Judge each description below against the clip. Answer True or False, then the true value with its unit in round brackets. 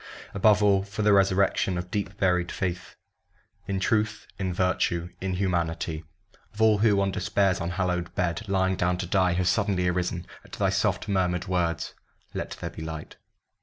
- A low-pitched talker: True (95 Hz)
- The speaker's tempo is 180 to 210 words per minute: False (165 wpm)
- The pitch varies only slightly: True (1.9 semitones)